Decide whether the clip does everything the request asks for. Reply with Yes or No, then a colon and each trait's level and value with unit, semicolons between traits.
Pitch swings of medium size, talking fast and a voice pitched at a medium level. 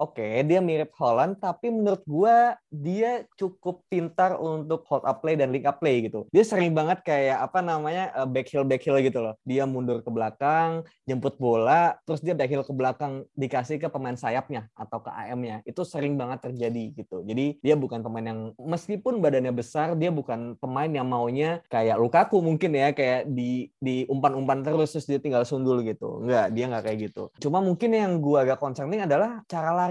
Yes: average, 4.8 semitones; fast, 195 wpm; medium, 145 Hz